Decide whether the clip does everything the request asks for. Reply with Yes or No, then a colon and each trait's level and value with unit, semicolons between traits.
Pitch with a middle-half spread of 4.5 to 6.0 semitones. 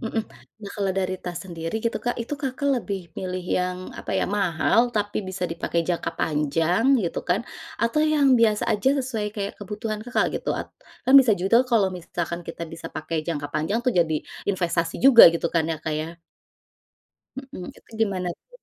Yes: average, 5.0 semitones